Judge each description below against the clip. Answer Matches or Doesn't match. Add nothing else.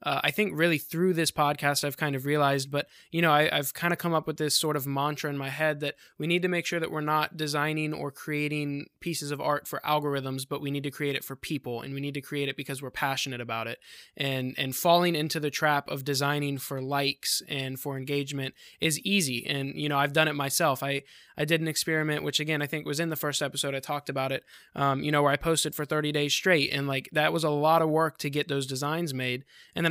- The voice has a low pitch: Doesn't match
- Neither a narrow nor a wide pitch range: Doesn't match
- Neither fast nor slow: Doesn't match